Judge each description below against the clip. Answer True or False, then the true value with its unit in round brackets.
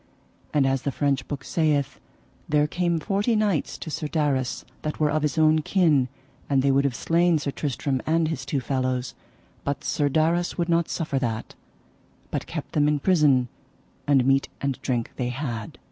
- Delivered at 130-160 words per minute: False (180 wpm)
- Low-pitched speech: False (145 Hz)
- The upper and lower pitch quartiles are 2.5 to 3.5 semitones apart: True (2.9 semitones)